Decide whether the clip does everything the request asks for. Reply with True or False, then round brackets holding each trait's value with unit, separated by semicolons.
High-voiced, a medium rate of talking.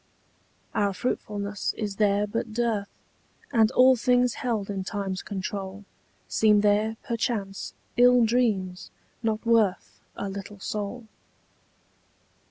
False (210 Hz; 110 wpm)